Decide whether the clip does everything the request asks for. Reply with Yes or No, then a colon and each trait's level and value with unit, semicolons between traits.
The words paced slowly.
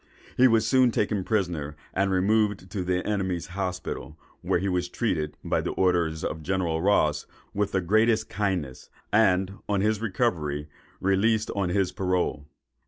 No: average, 160 wpm